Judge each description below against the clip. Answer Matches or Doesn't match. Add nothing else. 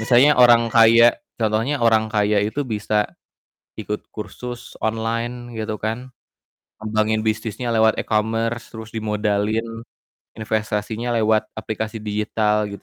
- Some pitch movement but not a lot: Doesn't match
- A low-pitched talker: Matches